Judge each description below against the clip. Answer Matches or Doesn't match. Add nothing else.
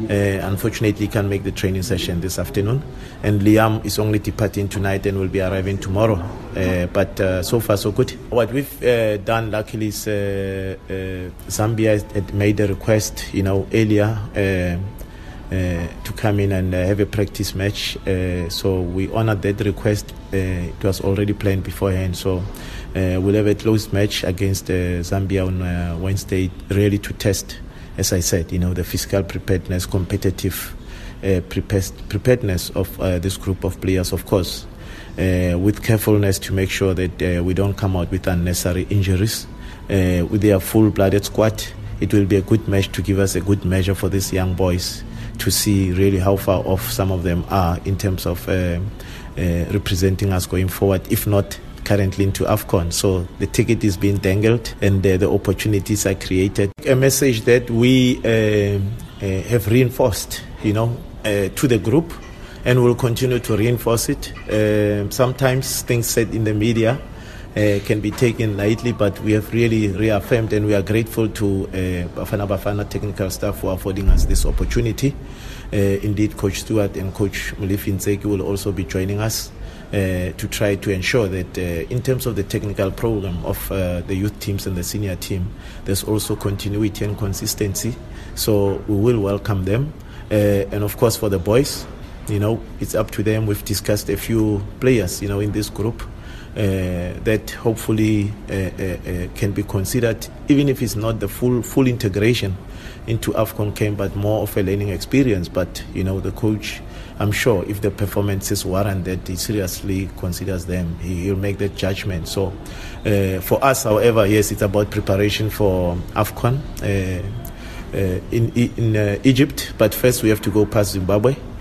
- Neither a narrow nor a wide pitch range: Doesn't match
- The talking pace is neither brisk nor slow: Matches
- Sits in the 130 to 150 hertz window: Doesn't match